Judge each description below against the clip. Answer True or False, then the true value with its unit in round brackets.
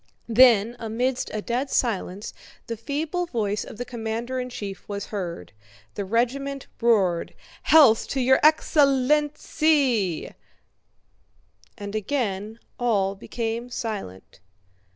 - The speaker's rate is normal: False (120 wpm)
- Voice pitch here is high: True (235 Hz)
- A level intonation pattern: False (4.3 semitones)